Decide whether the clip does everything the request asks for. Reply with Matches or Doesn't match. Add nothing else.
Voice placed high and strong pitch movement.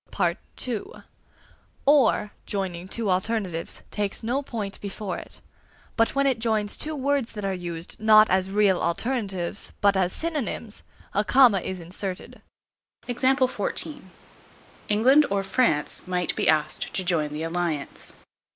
Doesn't match